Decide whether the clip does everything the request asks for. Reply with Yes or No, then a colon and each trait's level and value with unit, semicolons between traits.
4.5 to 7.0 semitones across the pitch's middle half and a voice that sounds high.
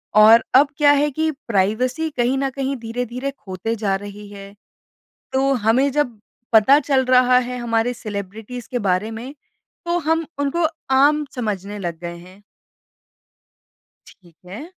Yes: average, 4.8 semitones; high, 245 Hz